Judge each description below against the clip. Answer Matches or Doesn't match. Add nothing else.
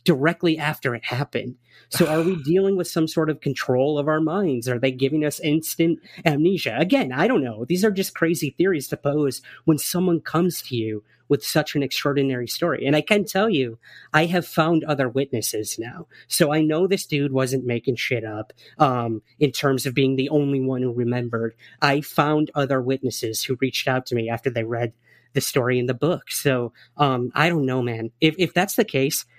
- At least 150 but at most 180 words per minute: Doesn't match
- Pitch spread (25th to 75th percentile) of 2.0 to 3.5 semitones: Doesn't match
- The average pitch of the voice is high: Doesn't match